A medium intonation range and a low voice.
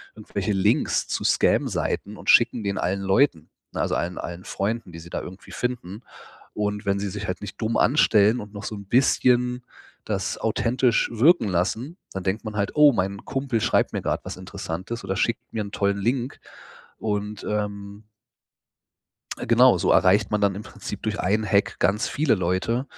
Yes: average, 3.2 semitones; low, 105 Hz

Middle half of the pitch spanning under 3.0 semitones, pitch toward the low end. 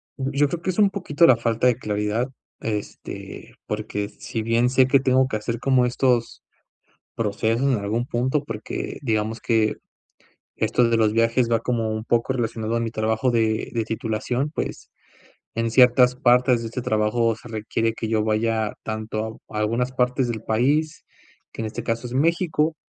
Yes: narrow, 2.4 semitones; low, 115 Hz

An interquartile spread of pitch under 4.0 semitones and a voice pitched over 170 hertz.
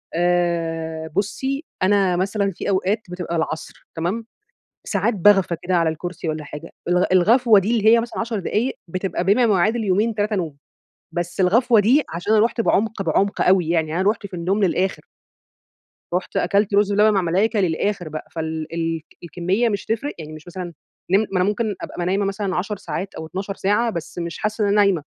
Yes: average, 3.5 semitones; high, 190 Hz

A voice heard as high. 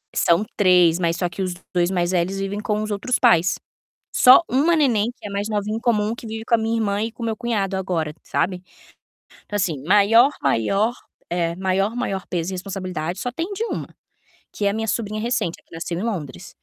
Yes: high, 200 Hz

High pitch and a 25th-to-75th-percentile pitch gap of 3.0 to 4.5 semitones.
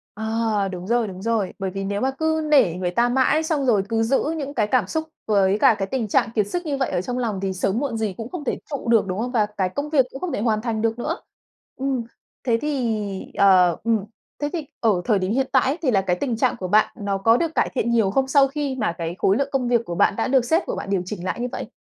No: high, 230 Hz; average, 5.2 semitones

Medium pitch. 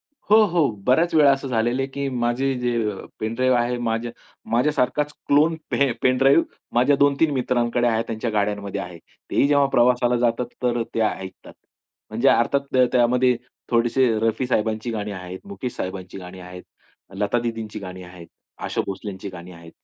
No: low, 120 Hz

